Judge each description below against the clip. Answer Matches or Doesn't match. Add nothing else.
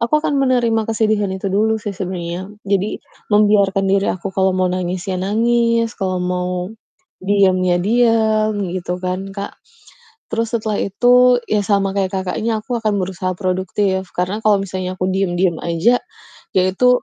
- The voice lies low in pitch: Doesn't match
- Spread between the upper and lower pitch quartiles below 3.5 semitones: Matches